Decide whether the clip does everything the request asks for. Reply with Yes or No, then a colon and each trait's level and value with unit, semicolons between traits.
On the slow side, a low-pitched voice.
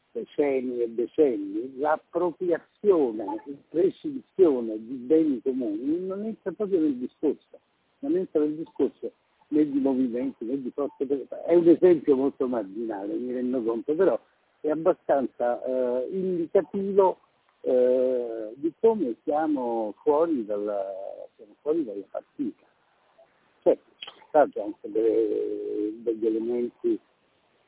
No: slow, 110 wpm; medium, 155 Hz